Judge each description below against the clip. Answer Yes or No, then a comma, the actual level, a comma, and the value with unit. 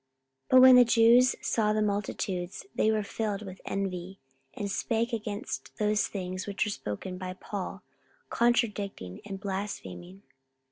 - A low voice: No, high, 205 Hz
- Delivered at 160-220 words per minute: No, average, 145 wpm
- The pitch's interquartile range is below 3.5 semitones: Yes, average, 2.8 semitones